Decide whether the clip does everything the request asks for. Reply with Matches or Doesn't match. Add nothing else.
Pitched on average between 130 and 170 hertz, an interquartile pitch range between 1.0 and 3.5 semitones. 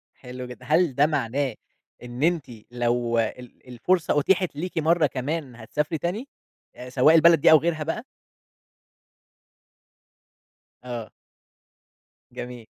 Doesn't match